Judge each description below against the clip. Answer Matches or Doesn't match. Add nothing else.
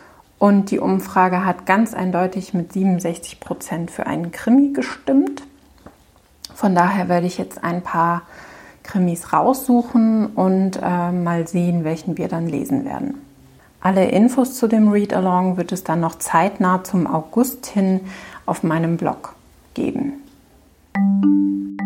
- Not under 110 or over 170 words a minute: Matches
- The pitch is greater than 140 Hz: Matches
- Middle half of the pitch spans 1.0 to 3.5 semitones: Doesn't match